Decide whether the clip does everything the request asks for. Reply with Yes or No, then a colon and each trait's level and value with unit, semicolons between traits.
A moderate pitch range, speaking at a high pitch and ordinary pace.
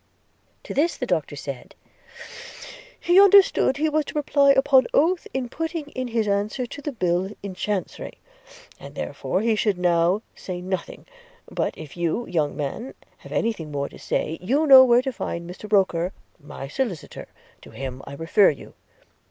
No: wide, 7.7 semitones; high, 210 Hz; average, 175 wpm